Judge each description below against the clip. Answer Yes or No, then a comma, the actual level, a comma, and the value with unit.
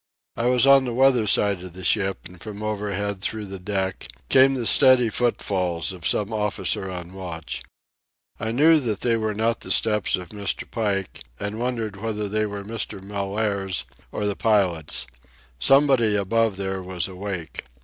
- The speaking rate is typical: Yes, average, 170 wpm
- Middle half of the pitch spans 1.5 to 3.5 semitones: Yes, average, 2.9 semitones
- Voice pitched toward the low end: Yes, low, 105 Hz